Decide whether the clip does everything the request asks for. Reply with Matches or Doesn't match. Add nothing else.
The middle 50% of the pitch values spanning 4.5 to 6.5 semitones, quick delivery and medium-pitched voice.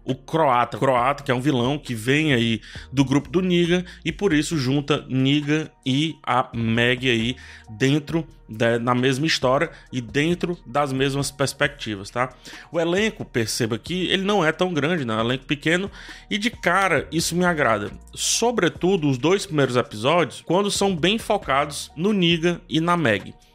Doesn't match